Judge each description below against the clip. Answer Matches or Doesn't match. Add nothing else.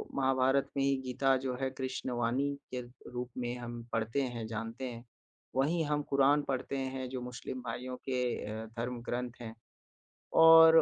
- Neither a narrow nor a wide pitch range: Doesn't match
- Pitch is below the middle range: Matches